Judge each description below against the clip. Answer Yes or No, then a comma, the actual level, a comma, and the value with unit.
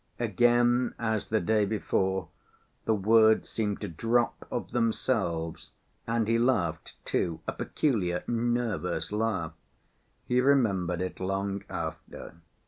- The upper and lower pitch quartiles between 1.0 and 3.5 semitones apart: No, average, 4.2 semitones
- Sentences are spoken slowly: Yes, slow, 120 wpm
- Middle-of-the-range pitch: No, low, 110 Hz